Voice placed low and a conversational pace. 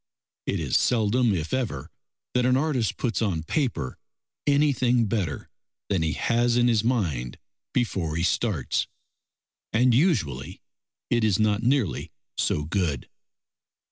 No: low, 110 Hz; slow, 130 wpm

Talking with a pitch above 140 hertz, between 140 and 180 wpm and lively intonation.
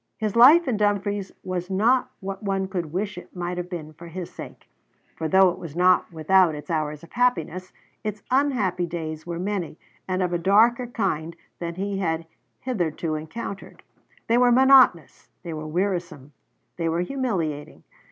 No: medium, 185 Hz; average, 170 wpm; average, 3.8 semitones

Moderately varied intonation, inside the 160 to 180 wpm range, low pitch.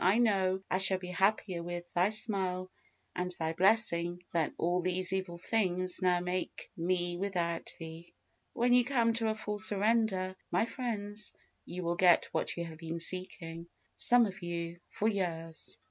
No: average, 3.2 semitones; average, 165 wpm; medium, 185 Hz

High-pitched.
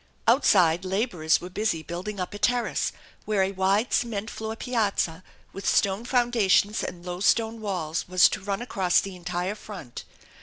Yes: high, 195 Hz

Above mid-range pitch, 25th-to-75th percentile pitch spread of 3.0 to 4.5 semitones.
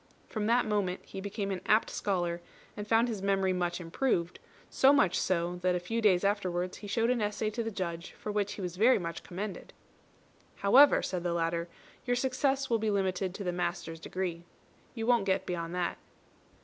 Yes: high, 195 Hz; average, 3.6 semitones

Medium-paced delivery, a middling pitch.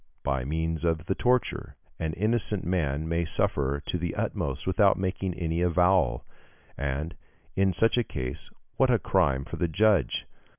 No: average, 160 wpm; very low, 85 Hz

